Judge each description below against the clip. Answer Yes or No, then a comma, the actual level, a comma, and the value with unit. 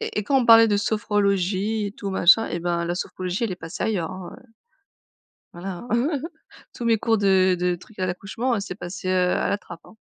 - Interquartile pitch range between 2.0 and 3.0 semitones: No, average, 3.5 semitones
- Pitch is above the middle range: Yes, high, 195 Hz